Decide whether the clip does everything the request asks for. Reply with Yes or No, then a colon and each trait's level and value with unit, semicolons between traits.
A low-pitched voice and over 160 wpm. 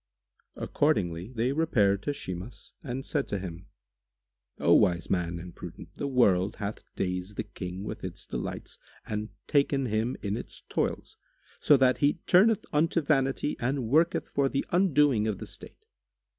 No: low, 120 Hz; average, 155 wpm